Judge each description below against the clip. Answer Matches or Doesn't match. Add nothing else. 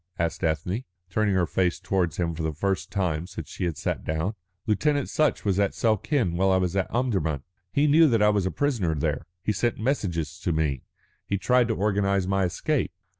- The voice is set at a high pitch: Doesn't match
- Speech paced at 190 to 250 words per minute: Matches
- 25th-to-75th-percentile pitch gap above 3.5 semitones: Matches